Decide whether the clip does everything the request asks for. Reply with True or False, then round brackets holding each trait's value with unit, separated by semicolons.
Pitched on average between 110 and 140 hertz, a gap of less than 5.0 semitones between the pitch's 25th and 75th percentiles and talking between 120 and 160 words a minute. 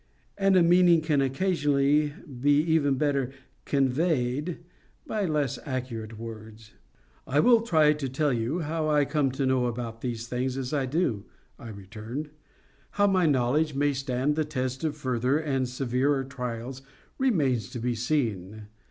True (135 Hz; 3.7 semitones; 150 wpm)